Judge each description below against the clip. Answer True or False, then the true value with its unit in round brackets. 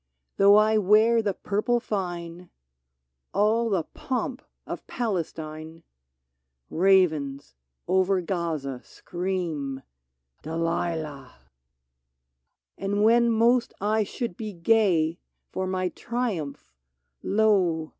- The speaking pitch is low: False (185 Hz)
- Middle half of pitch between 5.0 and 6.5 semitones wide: True (5.3 semitones)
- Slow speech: True (100 wpm)